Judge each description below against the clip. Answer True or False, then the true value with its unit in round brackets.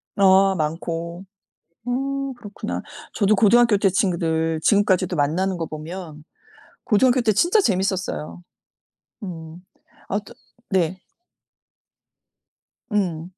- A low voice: False (190 Hz)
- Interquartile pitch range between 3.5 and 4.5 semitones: True (3.8 semitones)